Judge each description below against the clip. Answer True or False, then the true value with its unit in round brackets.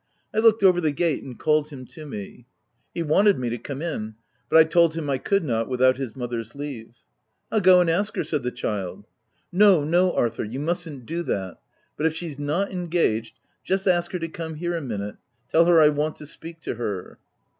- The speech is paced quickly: True (225 wpm)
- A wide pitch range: True (5.8 semitones)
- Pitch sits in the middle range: True (155 Hz)